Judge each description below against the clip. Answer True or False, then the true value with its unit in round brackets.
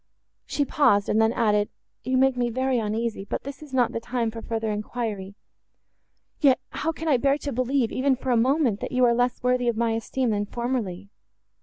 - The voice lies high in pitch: True (240 Hz)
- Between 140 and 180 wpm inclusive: False (200 wpm)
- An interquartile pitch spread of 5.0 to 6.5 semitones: False (2.9 semitones)